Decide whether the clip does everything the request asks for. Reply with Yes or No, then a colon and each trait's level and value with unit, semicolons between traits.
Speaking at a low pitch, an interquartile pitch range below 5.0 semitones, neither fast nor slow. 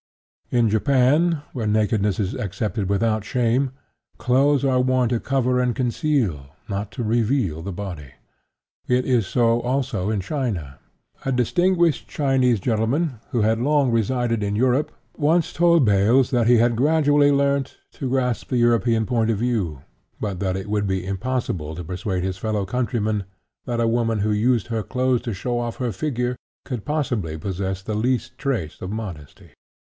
Yes: low, 115 Hz; average, 4.0 semitones; average, 165 wpm